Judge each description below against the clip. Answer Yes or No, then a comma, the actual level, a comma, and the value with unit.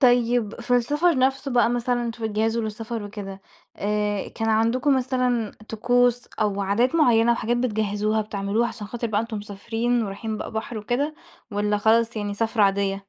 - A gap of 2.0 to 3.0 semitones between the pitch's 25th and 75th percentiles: Yes, average, 2.7 semitones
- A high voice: Yes, high, 225 Hz